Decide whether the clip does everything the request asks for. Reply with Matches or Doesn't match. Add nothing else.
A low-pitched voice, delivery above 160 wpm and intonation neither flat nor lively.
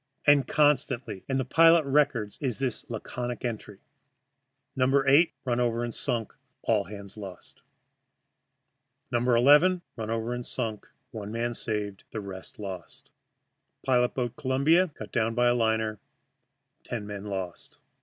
Doesn't match